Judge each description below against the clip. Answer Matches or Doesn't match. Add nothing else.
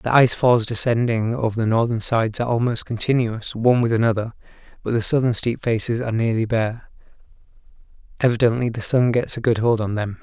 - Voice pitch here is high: Doesn't match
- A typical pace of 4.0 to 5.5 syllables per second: Doesn't match